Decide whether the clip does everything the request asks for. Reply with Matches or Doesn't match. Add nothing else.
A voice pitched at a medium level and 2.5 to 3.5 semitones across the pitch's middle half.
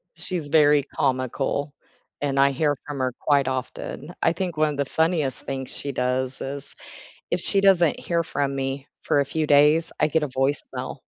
Matches